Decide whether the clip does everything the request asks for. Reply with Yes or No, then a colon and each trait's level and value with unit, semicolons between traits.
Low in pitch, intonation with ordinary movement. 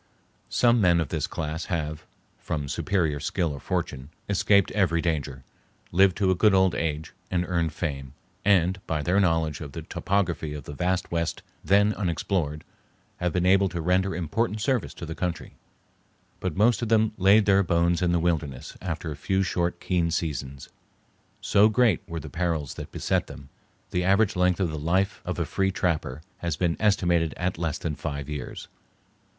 Yes: very low, 85 Hz; average, 3.5 semitones